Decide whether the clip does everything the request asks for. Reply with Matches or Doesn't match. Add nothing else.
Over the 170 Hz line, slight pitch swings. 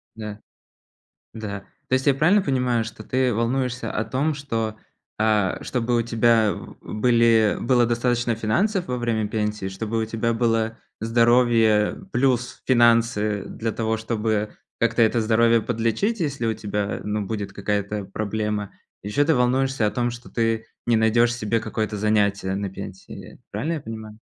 Doesn't match